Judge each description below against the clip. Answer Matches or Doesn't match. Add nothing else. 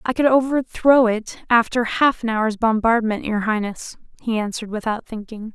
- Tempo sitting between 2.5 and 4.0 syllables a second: Doesn't match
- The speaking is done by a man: Doesn't match